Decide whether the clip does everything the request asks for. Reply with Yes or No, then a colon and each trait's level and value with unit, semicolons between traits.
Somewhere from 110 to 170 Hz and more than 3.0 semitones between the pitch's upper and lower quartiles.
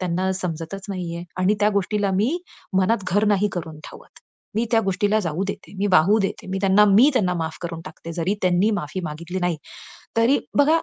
No: high, 190 Hz; average, 3.4 semitones